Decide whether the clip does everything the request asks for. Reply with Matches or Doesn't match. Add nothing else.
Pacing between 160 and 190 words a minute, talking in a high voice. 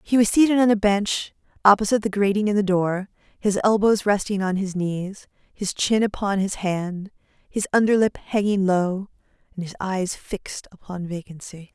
Matches